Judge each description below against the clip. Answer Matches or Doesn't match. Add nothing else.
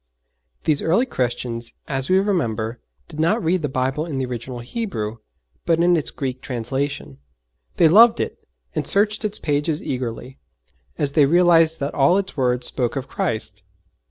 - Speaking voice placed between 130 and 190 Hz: Matches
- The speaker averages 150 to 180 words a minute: Matches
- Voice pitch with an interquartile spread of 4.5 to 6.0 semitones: Matches